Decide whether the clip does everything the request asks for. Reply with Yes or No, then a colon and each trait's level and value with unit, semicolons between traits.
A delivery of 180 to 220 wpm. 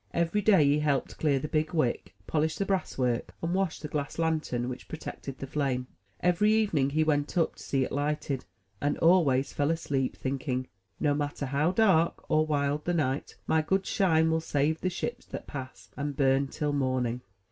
Yes: average, 190 wpm